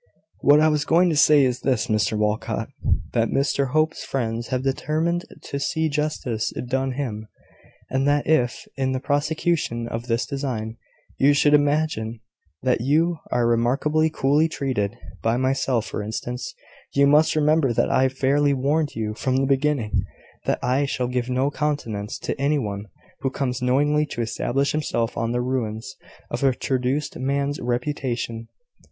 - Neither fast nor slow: Yes, average, 160 wpm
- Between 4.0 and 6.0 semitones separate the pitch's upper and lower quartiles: No, average, 3.6 semitones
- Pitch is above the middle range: No, low, 135 Hz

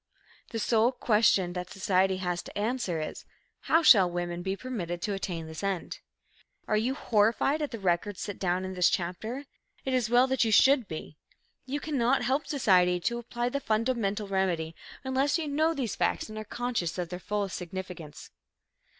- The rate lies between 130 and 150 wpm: No, average, 180 wpm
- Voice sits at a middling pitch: No, high, 210 Hz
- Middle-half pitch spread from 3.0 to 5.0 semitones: No, wide, 5.6 semitones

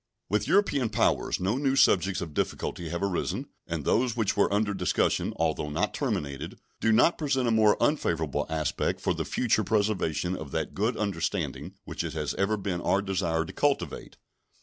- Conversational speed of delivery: Yes, average, 175 wpm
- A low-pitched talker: Yes, low, 100 Hz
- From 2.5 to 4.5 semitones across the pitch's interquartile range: No, average, 5.2 semitones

